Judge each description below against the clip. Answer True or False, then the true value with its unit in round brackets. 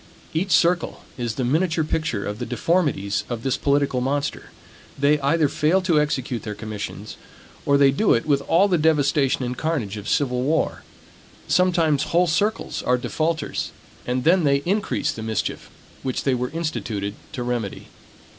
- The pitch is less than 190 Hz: True (140 Hz)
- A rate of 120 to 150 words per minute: False (165 wpm)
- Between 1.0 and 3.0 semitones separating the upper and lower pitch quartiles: False (4.7 semitones)